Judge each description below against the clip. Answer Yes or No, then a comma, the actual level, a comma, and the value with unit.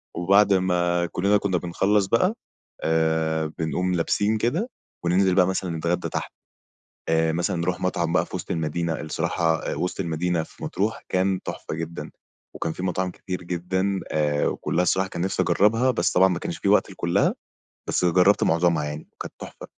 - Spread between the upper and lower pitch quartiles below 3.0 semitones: Yes, narrow, 2.5 semitones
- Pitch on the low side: Yes, very low, 90 Hz